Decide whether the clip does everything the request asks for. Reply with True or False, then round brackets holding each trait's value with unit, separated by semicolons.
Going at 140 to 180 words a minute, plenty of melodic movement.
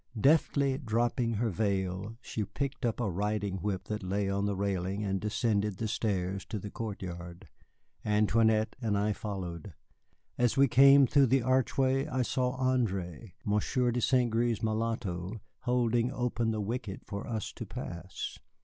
False (155 wpm; 3.7 semitones)